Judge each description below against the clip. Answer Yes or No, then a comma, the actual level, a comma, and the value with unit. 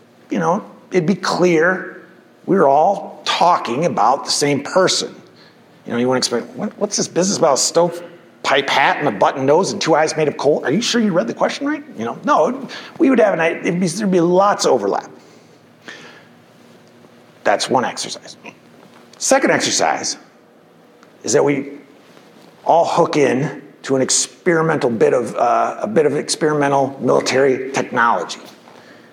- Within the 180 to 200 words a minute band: No, average, 165 wpm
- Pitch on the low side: No, medium, 170 Hz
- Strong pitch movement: Yes, wide, 5.8 semitones